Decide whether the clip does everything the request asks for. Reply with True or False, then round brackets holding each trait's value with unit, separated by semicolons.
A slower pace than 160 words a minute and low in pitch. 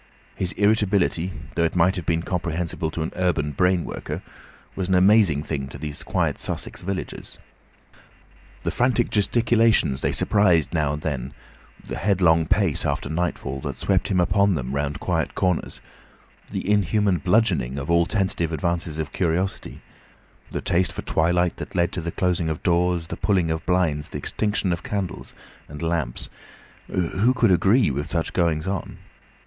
False (165 wpm; 85 Hz)